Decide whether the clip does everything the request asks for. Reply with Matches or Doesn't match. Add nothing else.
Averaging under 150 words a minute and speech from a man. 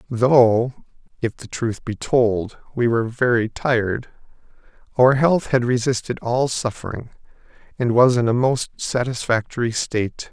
Matches